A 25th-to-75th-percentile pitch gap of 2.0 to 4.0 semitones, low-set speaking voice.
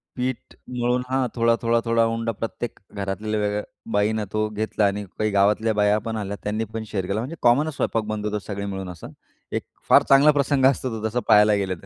Yes: narrow, 2.4 semitones; low, 110 Hz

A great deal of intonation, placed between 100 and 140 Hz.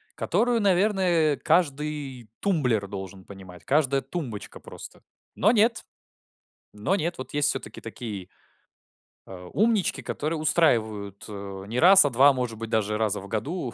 Yes: wide, 8.4 semitones; low, 135 Hz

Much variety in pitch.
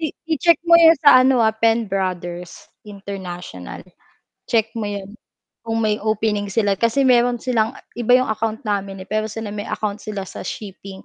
No: average, 2.9 semitones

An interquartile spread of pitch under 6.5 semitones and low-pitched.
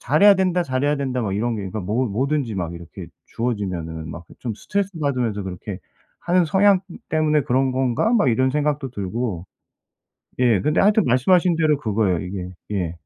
No: wide, 7.2 semitones; low, 125 Hz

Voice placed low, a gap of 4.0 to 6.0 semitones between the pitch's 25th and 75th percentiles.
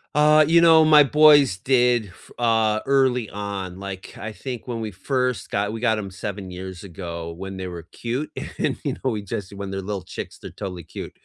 Yes: low, 105 Hz; average, 5.0 semitones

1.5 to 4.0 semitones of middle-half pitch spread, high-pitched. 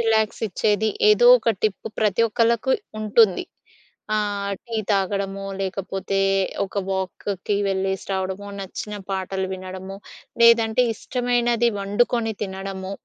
Yes: average, 2.8 semitones; high, 205 Hz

